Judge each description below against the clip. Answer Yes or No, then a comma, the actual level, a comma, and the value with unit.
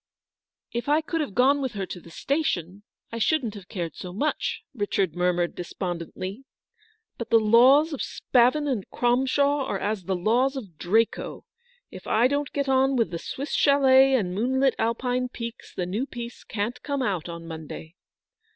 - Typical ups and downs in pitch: No, wide, 6.1 semitones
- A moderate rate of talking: Yes, average, 180 wpm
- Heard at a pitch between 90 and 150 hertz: No, high, 235 Hz